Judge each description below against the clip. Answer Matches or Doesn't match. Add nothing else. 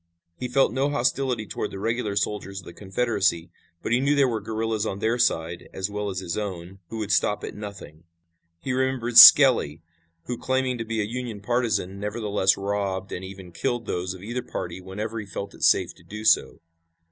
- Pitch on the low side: Matches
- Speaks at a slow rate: Doesn't match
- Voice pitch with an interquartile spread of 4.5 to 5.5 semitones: Doesn't match